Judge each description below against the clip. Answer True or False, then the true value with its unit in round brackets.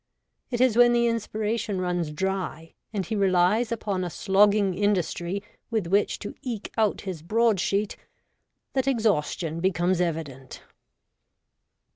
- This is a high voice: True (200 Hz)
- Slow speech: True (130 wpm)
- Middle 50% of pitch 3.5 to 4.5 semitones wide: True (3.8 semitones)